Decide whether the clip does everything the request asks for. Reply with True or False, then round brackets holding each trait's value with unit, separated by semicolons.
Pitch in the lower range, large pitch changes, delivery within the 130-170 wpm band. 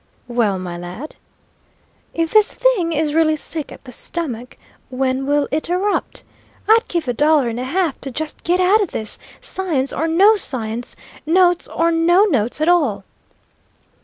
False (310 Hz; 5.7 semitones; 165 wpm)